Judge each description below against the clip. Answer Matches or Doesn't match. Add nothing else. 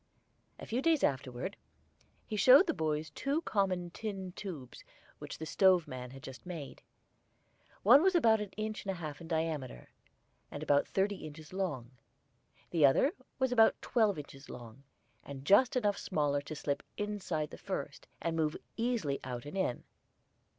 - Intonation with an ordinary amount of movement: Doesn't match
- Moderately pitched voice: Matches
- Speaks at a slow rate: Doesn't match